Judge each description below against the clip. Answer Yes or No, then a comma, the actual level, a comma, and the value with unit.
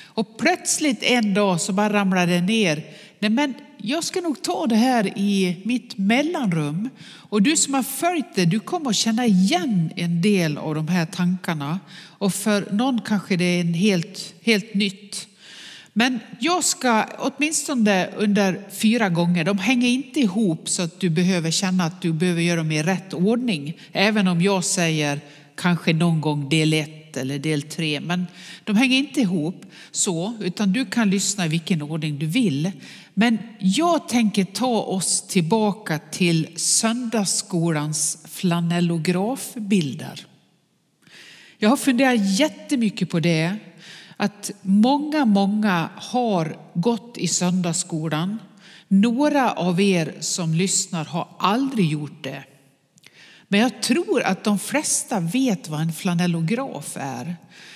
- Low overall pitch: No, high, 195 Hz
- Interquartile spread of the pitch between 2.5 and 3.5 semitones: No, average, 4.7 semitones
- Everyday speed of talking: Yes, average, 145 wpm